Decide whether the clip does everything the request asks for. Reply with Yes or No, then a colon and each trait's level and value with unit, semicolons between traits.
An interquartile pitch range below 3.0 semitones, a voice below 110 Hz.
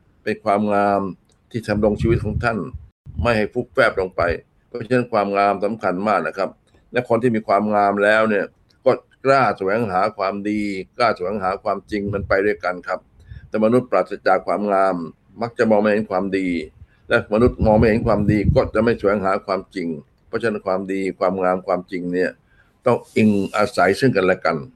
Yes: narrow, 2.6 semitones; low, 100 Hz